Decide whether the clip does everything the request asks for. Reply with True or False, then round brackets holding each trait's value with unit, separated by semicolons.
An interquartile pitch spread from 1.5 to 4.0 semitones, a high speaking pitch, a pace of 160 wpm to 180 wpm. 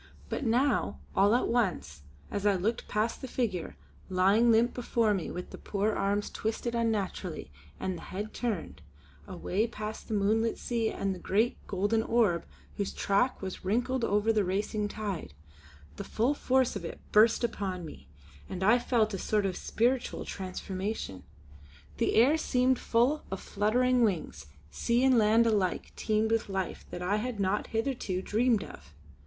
True (3.4 semitones; 215 Hz; 165 wpm)